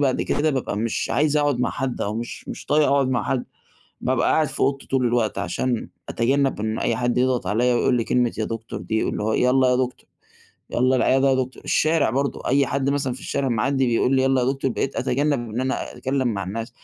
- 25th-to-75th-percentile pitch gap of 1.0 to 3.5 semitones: Yes, narrow, 2.5 semitones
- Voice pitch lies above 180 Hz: No, low, 130 Hz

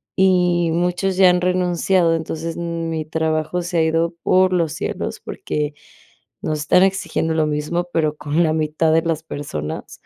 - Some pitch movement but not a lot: No, narrow, 2.1 semitones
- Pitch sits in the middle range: Yes, medium, 165 Hz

